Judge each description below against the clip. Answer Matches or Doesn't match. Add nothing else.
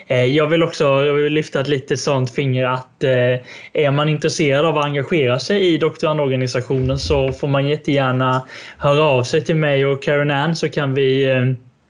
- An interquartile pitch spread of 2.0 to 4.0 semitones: Matches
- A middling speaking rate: Matches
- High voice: Doesn't match